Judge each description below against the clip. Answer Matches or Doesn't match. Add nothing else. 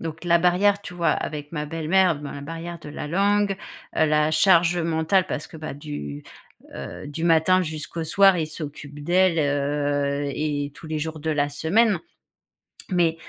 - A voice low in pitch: Doesn't match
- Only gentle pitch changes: Doesn't match